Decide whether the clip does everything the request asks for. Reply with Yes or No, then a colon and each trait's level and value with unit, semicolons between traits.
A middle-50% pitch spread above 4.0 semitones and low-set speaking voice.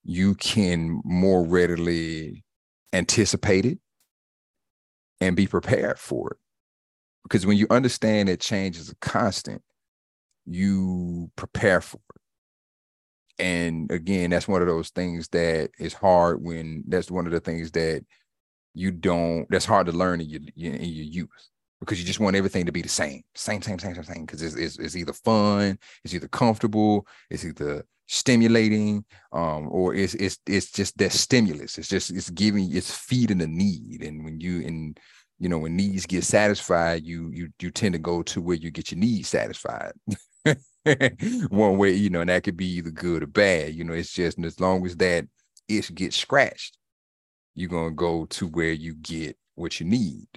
No: average, 3.3 semitones; very low, 90 Hz